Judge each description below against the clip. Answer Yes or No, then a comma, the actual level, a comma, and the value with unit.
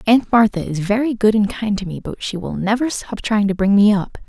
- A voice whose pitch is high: Yes, high, 210 Hz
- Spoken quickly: Yes, fast, 265 wpm